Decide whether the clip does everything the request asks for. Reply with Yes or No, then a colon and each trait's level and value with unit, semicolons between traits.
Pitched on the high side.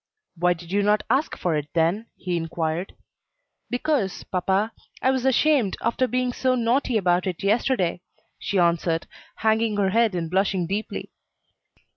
Yes: high, 200 Hz